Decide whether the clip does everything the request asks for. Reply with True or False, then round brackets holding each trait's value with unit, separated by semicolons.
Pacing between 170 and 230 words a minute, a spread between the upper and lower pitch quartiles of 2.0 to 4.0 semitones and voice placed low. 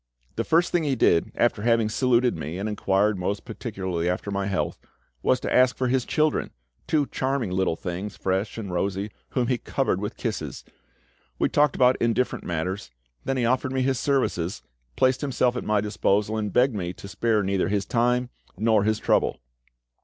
False (185 wpm; 4.6 semitones; 110 Hz)